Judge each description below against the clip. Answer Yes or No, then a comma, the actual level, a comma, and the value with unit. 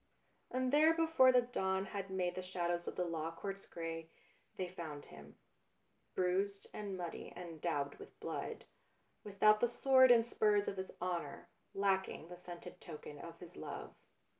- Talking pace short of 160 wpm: No, average, 165 wpm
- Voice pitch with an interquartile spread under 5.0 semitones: Yes, average, 3.7 semitones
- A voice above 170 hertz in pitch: Yes, medium, 185 Hz